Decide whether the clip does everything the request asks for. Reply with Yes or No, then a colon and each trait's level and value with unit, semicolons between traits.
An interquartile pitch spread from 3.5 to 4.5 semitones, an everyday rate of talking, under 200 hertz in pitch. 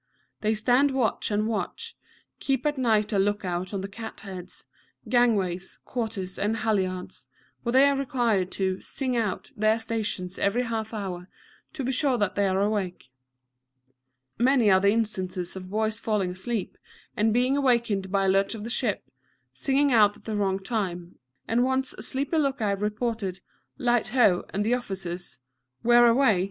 No: average, 4.1 semitones; average, 170 wpm; high, 215 Hz